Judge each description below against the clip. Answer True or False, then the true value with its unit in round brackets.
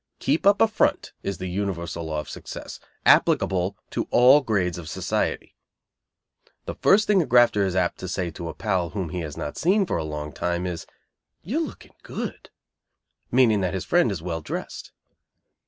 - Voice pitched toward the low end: True (95 Hz)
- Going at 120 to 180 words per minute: False (190 wpm)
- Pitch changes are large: True (6.3 semitones)